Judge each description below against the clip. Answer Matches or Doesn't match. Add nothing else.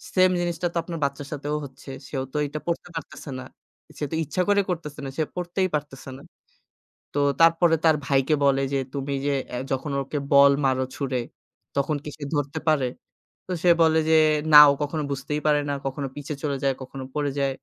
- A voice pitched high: Doesn't match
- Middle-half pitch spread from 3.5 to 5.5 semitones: Doesn't match